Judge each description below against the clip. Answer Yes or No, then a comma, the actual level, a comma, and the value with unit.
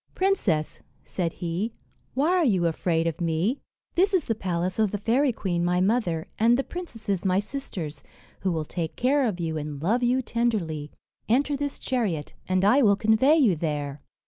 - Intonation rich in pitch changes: Yes, wide, 6.9 semitones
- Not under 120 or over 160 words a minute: No, average, 180 wpm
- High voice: Yes, high, 200 Hz